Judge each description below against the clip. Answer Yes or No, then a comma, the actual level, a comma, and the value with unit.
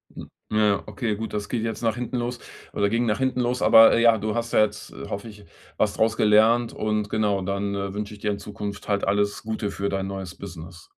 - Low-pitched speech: Yes, low, 105 Hz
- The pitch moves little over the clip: Yes, narrow, 2.0 semitones